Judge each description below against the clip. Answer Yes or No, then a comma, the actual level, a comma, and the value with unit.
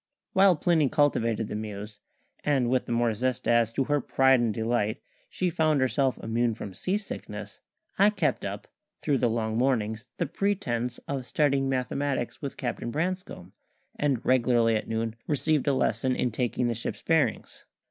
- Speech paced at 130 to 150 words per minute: No, average, 170 wpm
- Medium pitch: No, low, 125 Hz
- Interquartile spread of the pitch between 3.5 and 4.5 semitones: Yes, average, 4.2 semitones